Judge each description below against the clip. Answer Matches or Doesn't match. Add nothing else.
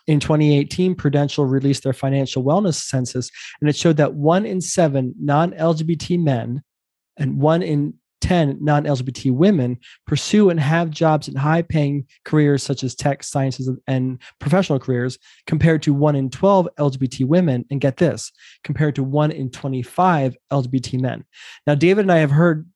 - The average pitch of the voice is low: Doesn't match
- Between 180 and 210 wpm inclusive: Doesn't match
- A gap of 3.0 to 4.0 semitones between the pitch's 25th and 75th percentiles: Matches